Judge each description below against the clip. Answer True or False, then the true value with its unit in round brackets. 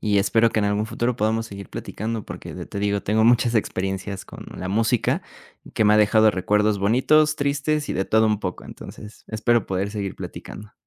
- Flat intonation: True (2.1 semitones)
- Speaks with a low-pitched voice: True (110 Hz)